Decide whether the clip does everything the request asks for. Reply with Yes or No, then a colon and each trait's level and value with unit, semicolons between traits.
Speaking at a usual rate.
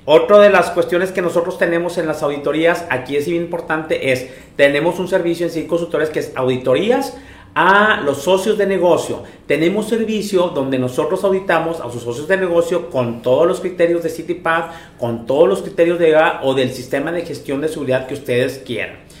No: fast, 195 wpm